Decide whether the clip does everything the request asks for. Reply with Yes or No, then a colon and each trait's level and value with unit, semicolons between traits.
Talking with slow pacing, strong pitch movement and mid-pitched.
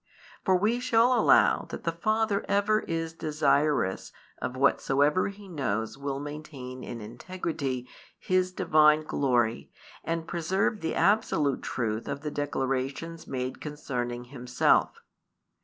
Yes: slow, 125 wpm; wide, 6.0 semitones; medium, 150 Hz